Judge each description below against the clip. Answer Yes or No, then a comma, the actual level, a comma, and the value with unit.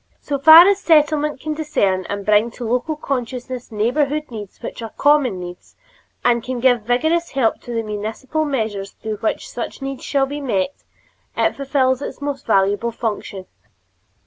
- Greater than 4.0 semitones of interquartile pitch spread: Yes, average, 4.9 semitones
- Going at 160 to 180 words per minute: Yes, average, 170 wpm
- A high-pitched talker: Yes, very high, 250 Hz